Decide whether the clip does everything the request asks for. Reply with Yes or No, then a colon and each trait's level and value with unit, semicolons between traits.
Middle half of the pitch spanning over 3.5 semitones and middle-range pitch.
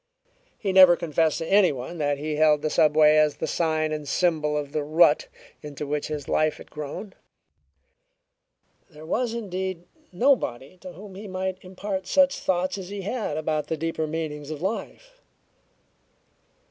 Yes: average, 3.9 semitones; medium, 165 Hz